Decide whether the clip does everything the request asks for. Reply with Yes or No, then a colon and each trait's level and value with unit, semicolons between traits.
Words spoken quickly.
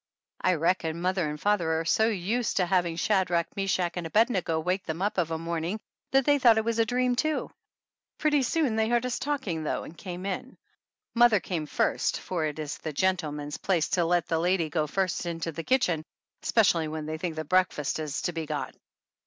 Yes: fast, 210 wpm